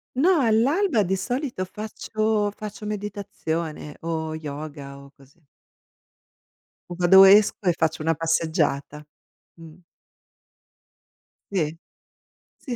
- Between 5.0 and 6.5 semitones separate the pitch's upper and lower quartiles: Yes, average, 5.3 semitones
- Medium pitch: Yes, medium, 180 Hz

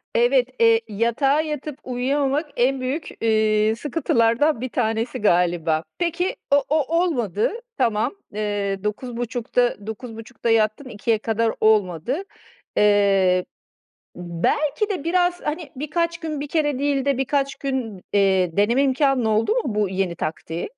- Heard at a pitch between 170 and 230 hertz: No, high, 245 Hz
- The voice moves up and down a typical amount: No, wide, 5.7 semitones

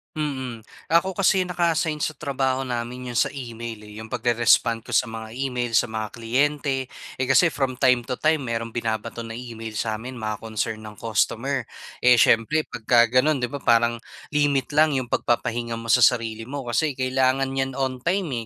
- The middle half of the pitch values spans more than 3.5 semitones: No, average, 3.1 semitones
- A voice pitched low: Yes, low, 125 Hz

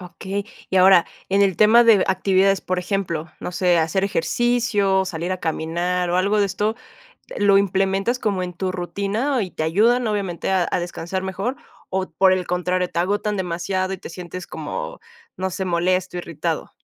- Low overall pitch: No, high, 190 Hz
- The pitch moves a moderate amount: No, narrow, 2.0 semitones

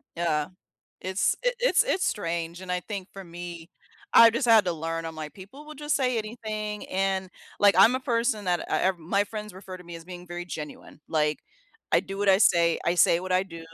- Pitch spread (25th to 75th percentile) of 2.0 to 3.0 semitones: No, average, 3.9 semitones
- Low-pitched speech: No, medium, 185 Hz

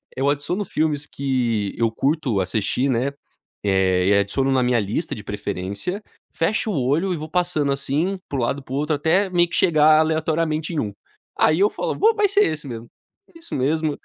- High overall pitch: No, medium, 145 Hz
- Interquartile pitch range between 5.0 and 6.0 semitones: Yes, wide, 5.6 semitones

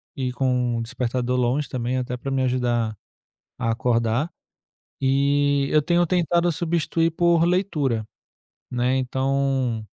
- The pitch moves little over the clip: No, average, 3.4 semitones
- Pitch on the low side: Yes, low, 130 Hz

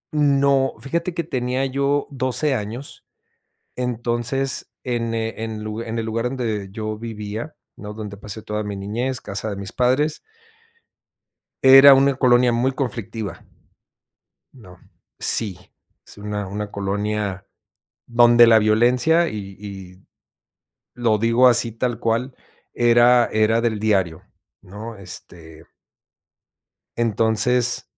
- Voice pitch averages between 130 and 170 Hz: No, low, 115 Hz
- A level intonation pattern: No, average, 3.2 semitones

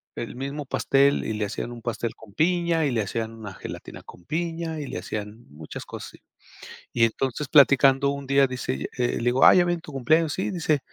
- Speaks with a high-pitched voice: No, low, 135 Hz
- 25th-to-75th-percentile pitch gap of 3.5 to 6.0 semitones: Yes, average, 5.2 semitones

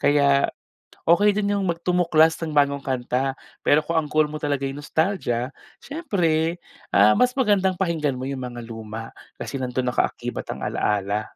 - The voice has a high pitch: No, medium, 145 Hz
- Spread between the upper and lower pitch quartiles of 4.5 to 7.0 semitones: Yes, average, 5.2 semitones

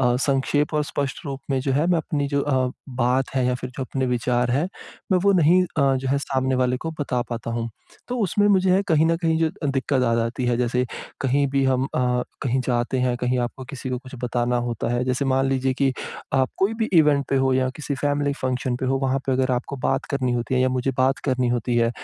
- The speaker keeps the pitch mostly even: Yes, narrow, 2.2 semitones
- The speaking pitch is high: No, low, 130 Hz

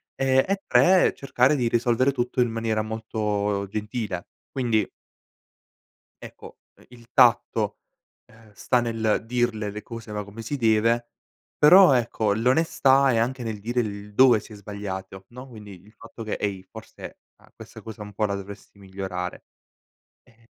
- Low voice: Yes, low, 110 Hz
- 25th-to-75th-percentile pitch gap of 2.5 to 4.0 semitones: Yes, average, 2.9 semitones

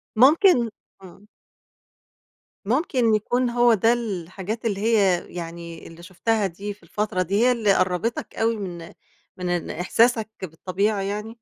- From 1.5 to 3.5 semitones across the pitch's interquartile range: No, average, 4.1 semitones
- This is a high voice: Yes, high, 205 Hz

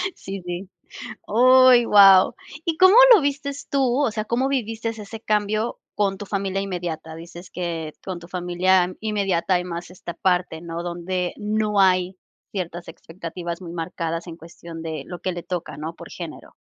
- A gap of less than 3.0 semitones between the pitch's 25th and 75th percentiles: No, average, 3.6 semitones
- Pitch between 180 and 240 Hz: Yes, medium, 185 Hz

